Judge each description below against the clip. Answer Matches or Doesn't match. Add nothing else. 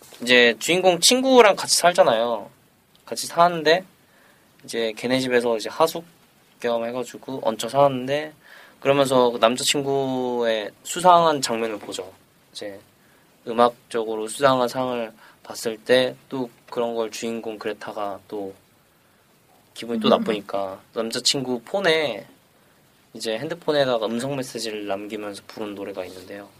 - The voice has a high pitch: Doesn't match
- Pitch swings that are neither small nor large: Matches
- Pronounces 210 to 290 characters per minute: Matches